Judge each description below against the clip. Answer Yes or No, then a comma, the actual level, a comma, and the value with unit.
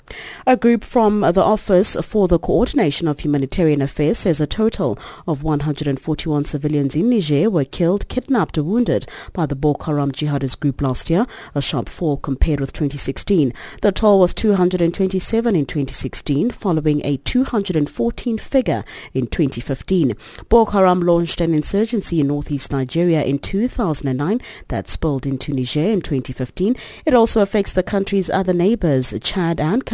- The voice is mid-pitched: Yes, medium, 165 Hz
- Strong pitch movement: Yes, wide, 6.2 semitones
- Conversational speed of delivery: Yes, average, 150 wpm